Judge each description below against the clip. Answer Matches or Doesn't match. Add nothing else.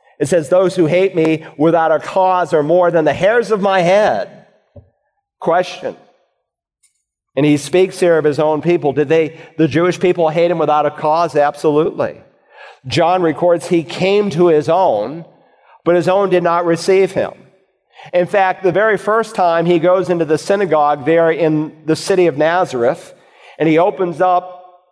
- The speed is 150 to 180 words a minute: Matches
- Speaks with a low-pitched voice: Doesn't match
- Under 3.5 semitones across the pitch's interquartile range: Matches